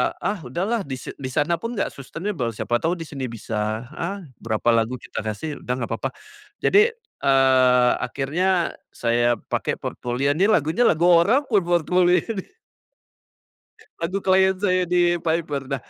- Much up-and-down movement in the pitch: Yes, wide, 6.5 semitones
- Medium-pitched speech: Yes, medium, 155 Hz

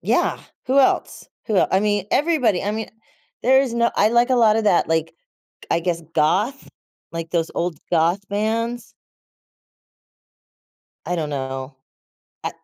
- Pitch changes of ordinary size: No, wide, 5.9 semitones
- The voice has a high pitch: Yes, high, 205 Hz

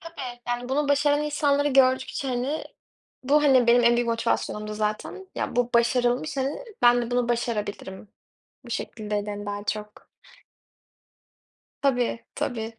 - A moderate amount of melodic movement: Yes, average, 3.4 semitones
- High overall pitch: Yes, high, 245 Hz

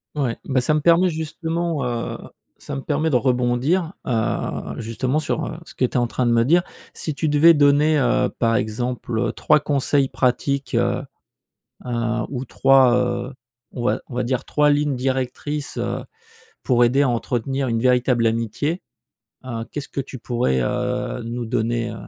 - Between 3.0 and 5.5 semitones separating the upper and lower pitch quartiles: Yes, average, 3.3 semitones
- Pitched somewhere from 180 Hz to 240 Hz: No, low, 130 Hz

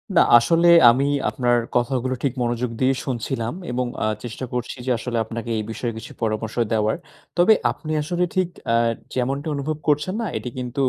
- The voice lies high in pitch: No, low, 125 Hz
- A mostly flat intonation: No, average, 3.2 semitones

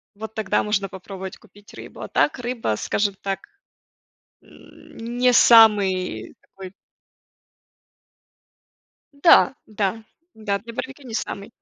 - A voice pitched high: Yes, high, 210 Hz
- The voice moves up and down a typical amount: Yes, average, 3.1 semitones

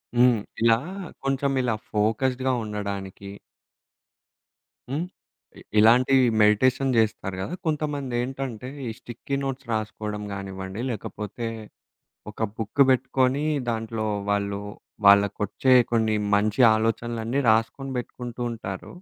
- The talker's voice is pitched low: Yes, low, 115 Hz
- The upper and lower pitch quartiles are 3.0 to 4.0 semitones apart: Yes, average, 3.7 semitones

